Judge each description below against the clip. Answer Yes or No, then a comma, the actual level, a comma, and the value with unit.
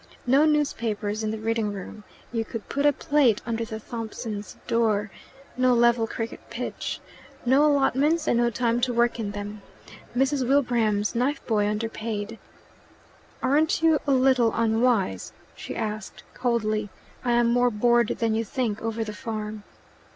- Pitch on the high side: Yes, high, 230 Hz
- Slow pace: No, average, 150 wpm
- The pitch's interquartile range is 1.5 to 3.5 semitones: Yes, average, 2.8 semitones